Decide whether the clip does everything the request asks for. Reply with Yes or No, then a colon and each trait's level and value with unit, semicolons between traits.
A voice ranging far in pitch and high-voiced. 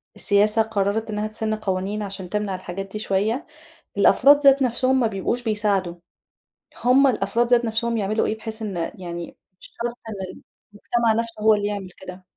No: average, 2.8 semitones; high, 215 Hz